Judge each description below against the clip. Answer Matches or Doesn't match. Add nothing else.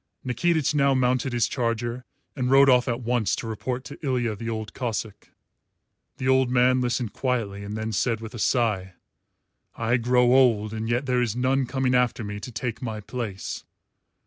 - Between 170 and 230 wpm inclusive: Matches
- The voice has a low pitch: Matches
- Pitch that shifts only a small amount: Matches